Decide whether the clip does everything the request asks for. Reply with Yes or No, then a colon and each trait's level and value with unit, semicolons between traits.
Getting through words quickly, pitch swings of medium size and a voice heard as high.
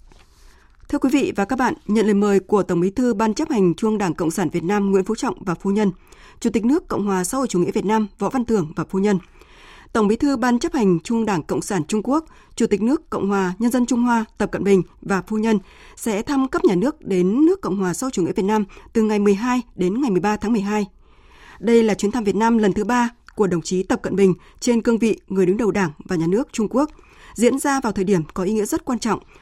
Yes: fast, 270 wpm; average, 3.9 semitones; high, 210 Hz